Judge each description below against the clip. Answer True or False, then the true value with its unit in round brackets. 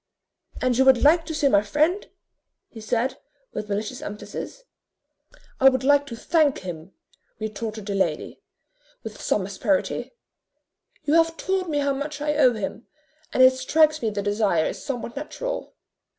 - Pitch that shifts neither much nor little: False (5.9 semitones)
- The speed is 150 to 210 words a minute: True (160 wpm)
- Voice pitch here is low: False (260 Hz)